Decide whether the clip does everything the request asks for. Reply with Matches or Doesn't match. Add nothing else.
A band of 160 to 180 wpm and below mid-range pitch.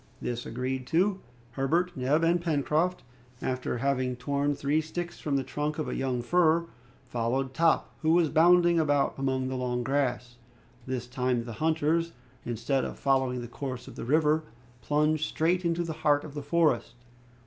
Doesn't match